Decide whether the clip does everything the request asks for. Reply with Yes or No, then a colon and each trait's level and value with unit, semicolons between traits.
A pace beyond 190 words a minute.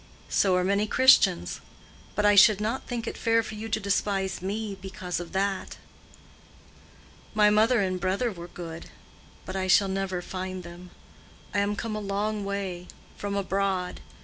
No: average, 160 wpm